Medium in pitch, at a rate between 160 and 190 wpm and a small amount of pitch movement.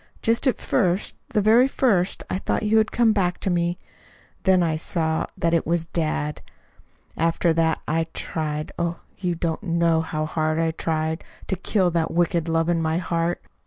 Yes: medium, 170 Hz; average, 180 wpm; narrow, 2.3 semitones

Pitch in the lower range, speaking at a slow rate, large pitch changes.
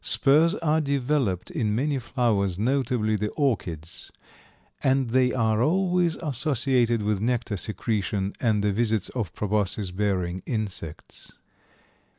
No: low, 115 Hz; slow, 120 wpm; average, 4.7 semitones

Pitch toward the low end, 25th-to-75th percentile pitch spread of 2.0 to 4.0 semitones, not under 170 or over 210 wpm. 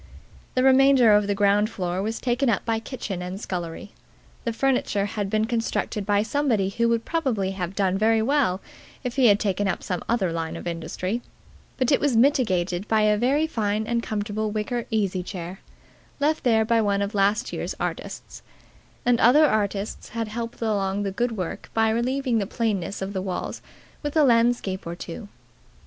No: high, 215 Hz; average, 3.4 semitones; average, 185 wpm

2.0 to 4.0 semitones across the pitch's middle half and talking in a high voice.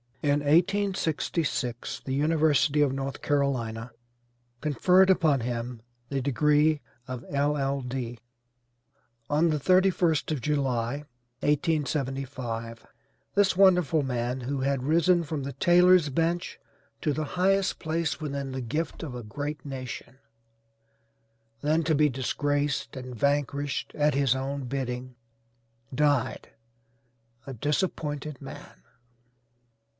No: average, 3.2 semitones; medium, 145 Hz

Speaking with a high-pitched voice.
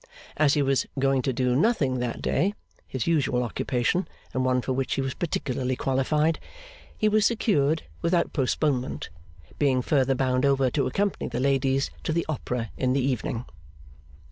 No: low, 135 Hz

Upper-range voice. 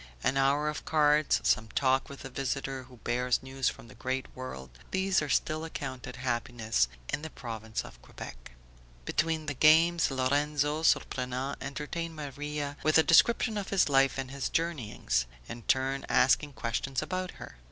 No: low, 135 Hz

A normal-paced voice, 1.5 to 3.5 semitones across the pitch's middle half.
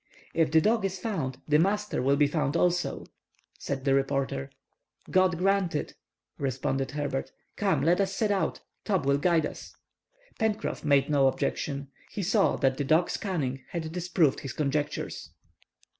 No: average, 160 wpm; average, 5.3 semitones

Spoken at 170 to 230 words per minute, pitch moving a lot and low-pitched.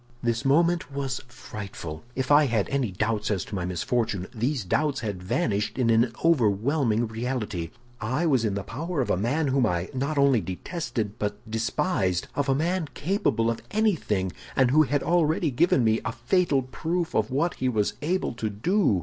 Yes: average, 180 wpm; wide, 5.7 semitones; low, 125 Hz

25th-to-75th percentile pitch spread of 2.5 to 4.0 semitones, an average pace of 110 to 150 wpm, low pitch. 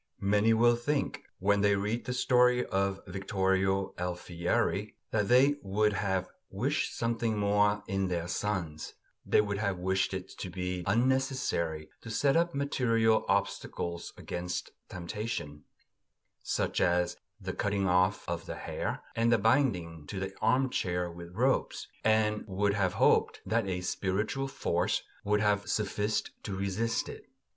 Yes: average, 3.7 semitones; average, 145 wpm; low, 100 Hz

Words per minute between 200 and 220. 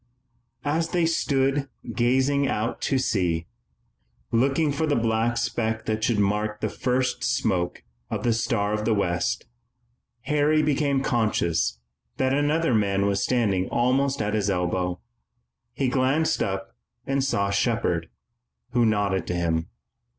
No: average, 140 wpm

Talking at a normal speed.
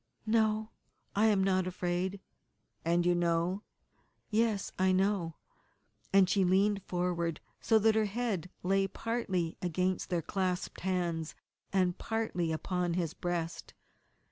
No: slow, 130 wpm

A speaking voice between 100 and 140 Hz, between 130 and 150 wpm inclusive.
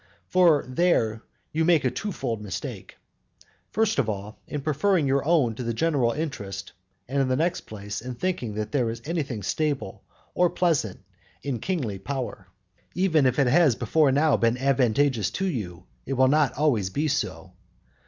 No: low, 135 Hz; average, 175 wpm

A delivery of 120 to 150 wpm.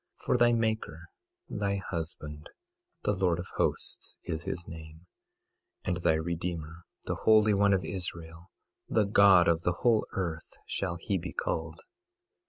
Yes: average, 145 wpm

